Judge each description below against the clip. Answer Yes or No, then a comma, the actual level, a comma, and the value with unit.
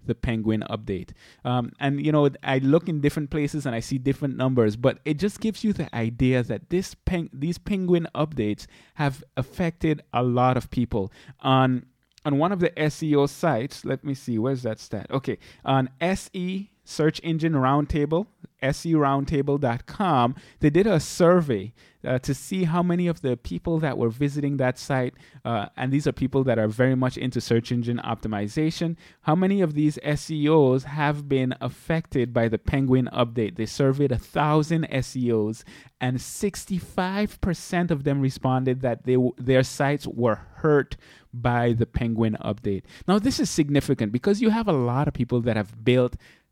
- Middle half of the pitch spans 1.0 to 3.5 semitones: No, average, 4.4 semitones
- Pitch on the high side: No, low, 135 Hz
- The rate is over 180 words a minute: No, average, 170 wpm